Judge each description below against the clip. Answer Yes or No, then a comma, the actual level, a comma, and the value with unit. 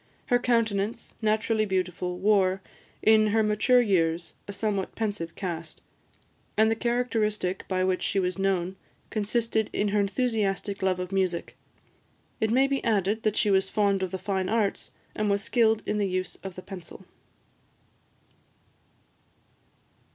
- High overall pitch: Yes, high, 200 Hz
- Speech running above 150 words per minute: No, average, 145 wpm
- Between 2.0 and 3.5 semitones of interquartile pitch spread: Yes, average, 2.7 semitones